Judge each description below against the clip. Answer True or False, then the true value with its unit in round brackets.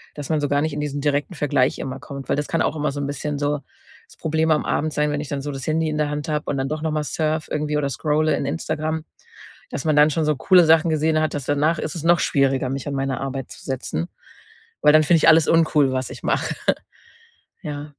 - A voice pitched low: False (150 Hz)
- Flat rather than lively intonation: True (1.8 semitones)